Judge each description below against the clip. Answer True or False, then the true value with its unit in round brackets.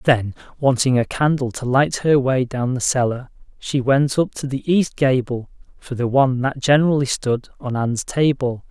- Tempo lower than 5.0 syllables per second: True (4.8 syllables/s)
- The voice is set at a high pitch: False (130 Hz)